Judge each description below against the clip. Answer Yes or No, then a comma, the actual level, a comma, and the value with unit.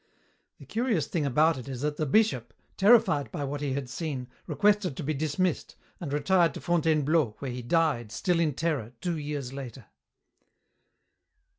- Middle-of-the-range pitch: Yes, medium, 150 Hz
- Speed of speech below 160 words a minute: No, average, 165 wpm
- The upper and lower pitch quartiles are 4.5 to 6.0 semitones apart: No, average, 4.0 semitones